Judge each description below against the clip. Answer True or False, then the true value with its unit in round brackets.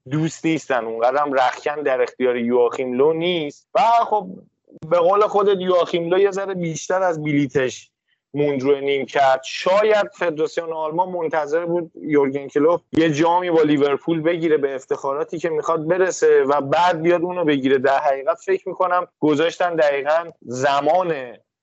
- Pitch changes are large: False (4.0 semitones)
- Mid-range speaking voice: True (160 Hz)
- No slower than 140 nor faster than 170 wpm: True (150 wpm)